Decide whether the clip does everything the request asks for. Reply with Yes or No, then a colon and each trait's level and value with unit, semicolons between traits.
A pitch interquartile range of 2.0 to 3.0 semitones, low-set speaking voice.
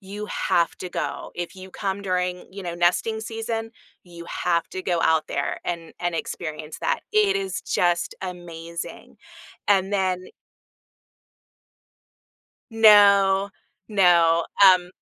No: average, 2.7 semitones; medium, 185 Hz